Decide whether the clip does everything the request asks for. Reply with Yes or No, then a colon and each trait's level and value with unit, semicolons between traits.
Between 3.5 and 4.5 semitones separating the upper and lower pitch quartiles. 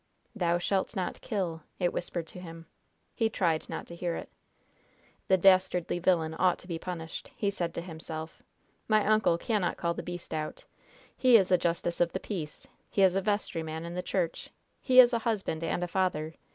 No: narrow, 2.6 semitones